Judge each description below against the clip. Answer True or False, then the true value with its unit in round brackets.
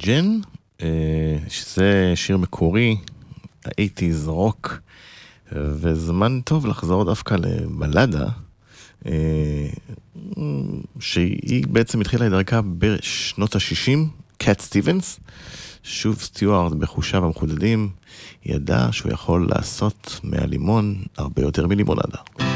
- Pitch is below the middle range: True (100 Hz)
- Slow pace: True (85 wpm)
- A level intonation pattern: False (5.3 semitones)